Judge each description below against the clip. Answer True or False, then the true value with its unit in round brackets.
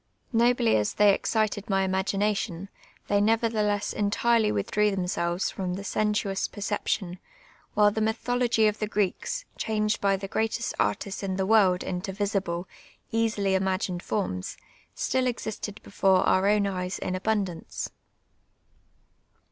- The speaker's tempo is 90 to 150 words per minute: True (135 wpm)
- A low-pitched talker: False (205 Hz)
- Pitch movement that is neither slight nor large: False (2.3 semitones)